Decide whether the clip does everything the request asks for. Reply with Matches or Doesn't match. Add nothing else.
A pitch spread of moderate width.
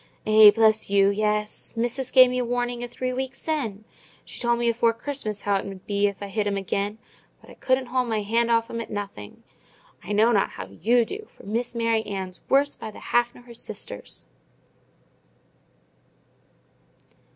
Matches